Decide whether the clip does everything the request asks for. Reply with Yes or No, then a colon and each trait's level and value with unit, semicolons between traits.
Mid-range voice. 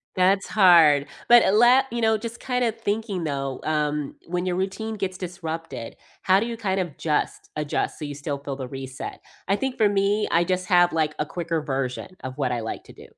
Yes: medium, 175 Hz